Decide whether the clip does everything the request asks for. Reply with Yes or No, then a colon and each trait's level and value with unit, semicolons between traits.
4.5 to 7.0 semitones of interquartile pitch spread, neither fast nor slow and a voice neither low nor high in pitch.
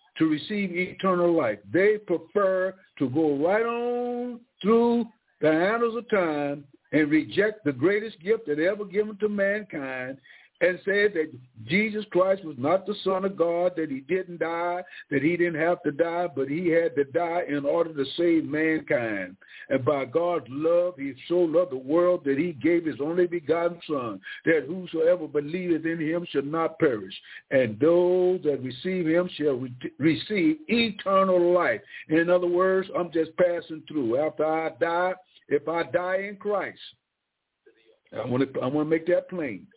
No: average, 3.7 semitones; average, 165 wpm; medium, 175 Hz